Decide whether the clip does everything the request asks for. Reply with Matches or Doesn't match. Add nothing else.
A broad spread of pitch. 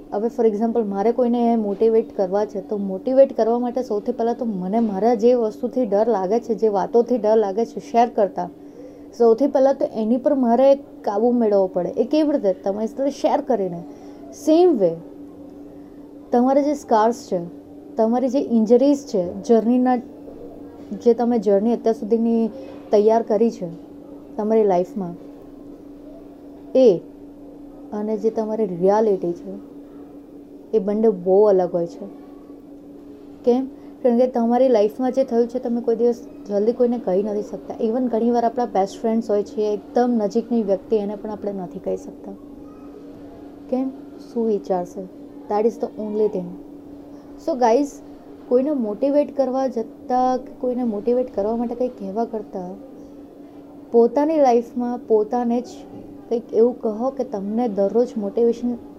Doesn't match